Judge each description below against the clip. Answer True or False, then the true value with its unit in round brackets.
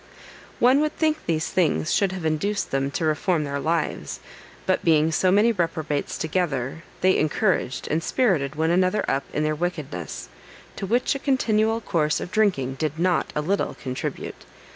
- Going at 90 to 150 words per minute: False (165 wpm)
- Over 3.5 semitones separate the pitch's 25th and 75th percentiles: True (4.9 semitones)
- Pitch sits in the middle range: True (165 Hz)